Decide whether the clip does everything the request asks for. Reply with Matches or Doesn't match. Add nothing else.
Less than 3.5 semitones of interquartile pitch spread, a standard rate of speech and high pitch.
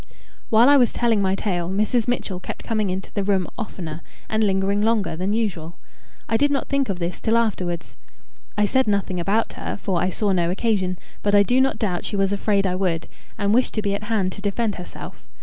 Doesn't match